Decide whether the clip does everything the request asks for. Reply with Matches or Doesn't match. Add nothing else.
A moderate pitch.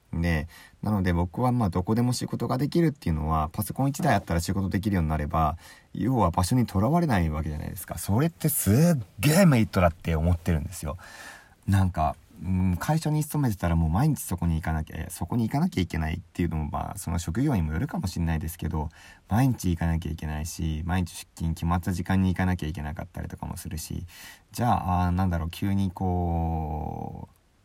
Doesn't match